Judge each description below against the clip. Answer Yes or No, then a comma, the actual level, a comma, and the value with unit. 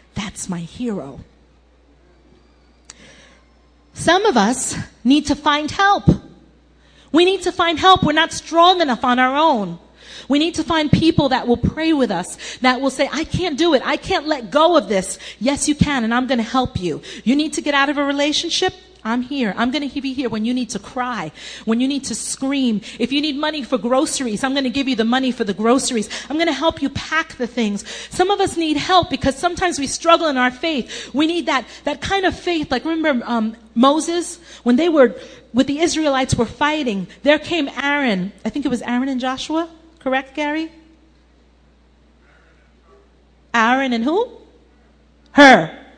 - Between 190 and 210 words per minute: Yes, average, 195 wpm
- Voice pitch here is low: No, very high, 270 Hz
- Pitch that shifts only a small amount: No, average, 5.3 semitones